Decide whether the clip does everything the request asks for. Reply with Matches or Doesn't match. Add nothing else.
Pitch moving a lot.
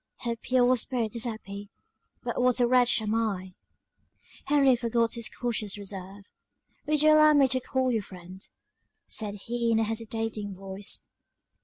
Doesn't match